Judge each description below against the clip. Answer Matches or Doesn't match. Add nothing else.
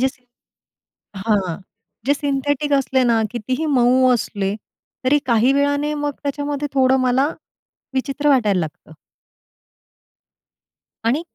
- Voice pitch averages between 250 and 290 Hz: Matches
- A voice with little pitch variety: Doesn't match